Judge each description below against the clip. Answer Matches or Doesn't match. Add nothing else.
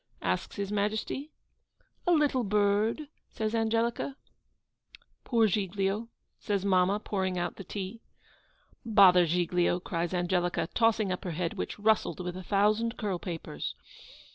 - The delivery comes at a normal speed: Doesn't match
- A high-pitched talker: Matches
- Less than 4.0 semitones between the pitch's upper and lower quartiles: Matches